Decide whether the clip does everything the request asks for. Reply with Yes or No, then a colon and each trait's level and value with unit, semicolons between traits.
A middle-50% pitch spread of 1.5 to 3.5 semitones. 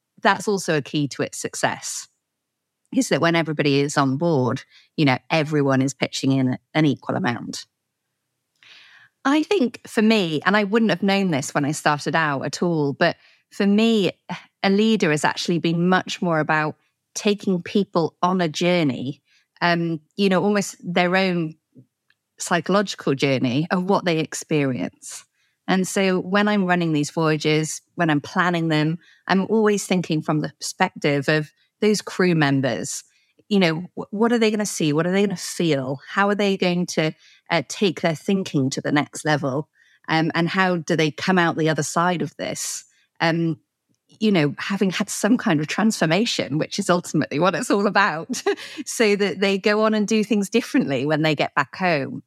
No: average, 4.7 semitones